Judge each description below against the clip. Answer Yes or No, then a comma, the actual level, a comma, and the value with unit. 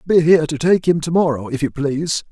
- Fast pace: Yes, fast, 260 wpm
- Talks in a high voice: No, medium, 155 Hz